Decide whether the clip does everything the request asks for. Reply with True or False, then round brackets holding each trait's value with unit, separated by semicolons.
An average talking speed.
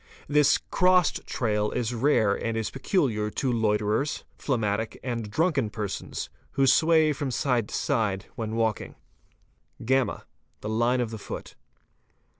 True (145 wpm)